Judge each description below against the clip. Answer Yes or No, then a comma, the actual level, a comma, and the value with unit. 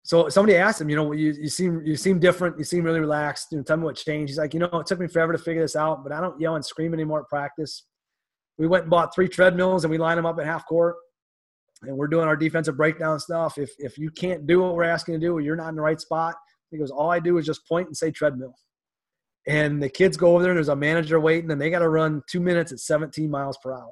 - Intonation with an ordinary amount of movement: No, narrow, 2.0 semitones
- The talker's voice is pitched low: No, medium, 160 Hz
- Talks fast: Yes, fast, 290 wpm